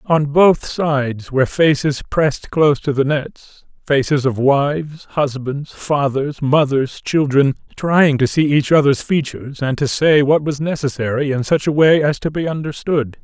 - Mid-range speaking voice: Yes, medium, 145 Hz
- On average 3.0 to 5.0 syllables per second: Yes, 4.4 syllables/s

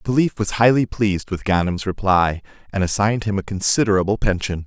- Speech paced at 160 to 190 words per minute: Yes, average, 180 wpm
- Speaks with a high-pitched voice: No, low, 100 Hz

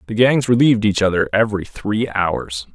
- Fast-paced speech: No, average, 175 wpm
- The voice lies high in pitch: No, low, 105 Hz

